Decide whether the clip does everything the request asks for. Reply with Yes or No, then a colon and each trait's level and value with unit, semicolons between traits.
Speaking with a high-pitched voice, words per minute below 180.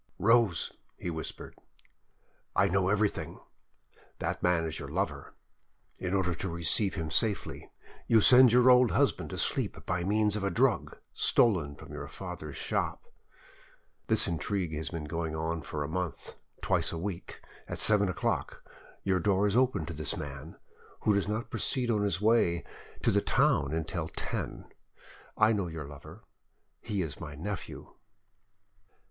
No: very low, 90 Hz; average, 155 wpm